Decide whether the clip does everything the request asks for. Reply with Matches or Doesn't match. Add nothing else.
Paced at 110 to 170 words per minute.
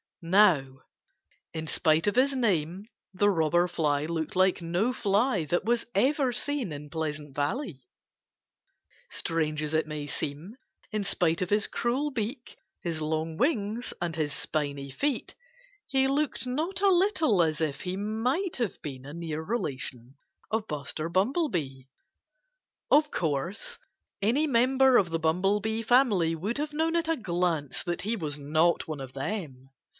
Matches